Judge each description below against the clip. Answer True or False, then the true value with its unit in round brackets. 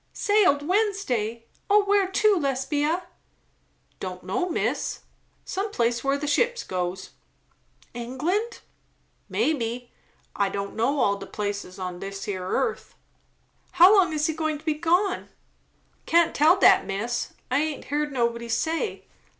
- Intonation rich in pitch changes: True (7.7 semitones)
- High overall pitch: True (290 Hz)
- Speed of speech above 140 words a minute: False (135 wpm)